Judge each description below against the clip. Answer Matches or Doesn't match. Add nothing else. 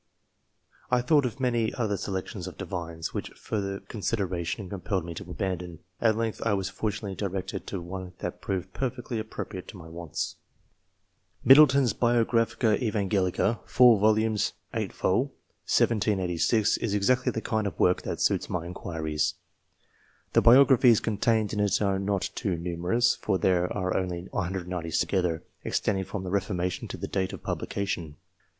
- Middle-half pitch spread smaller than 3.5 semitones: Doesn't match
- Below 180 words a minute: Matches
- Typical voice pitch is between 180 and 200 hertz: Doesn't match